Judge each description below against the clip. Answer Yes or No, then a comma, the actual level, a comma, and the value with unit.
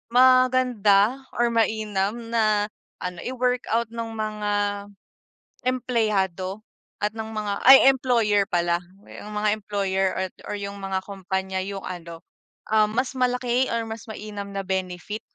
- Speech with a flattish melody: No, average, 3.2 semitones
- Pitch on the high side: Yes, high, 210 Hz